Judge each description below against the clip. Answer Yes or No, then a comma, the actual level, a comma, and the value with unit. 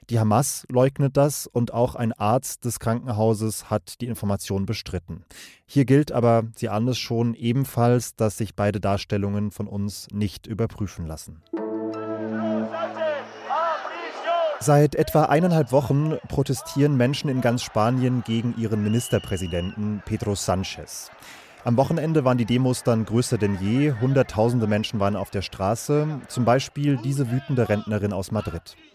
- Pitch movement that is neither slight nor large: Yes, average, 3.7 semitones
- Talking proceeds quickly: No, average, 135 wpm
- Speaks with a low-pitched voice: Yes, low, 115 Hz